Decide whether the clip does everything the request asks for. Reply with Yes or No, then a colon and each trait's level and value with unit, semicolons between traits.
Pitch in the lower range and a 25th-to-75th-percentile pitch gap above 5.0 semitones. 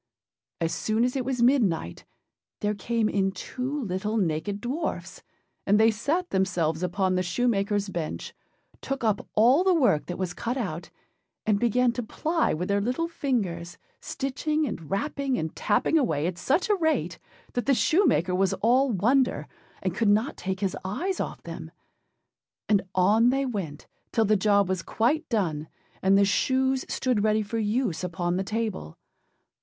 No: high, 215 Hz; wide, 5.5 semitones